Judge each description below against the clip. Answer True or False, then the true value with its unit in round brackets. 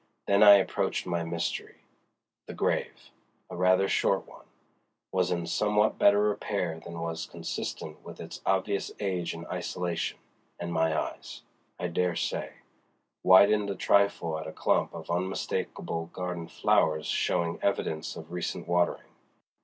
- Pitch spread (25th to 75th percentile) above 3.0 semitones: False (2.6 semitones)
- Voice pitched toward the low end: True (90 Hz)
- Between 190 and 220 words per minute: False (135 wpm)